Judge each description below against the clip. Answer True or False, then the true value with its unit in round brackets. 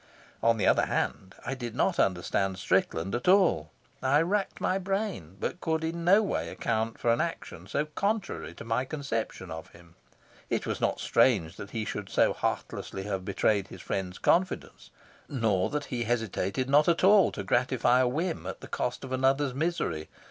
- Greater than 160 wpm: True (185 wpm)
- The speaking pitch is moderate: False (125 Hz)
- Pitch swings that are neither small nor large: False (8.7 semitones)